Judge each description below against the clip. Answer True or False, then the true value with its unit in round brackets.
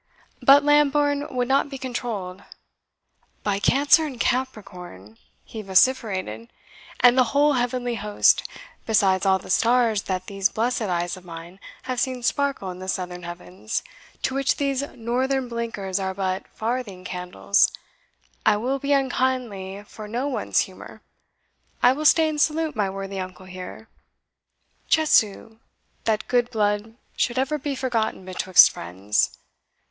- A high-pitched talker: True (225 Hz)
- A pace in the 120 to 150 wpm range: True (140 wpm)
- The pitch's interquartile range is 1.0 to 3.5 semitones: False (5.6 semitones)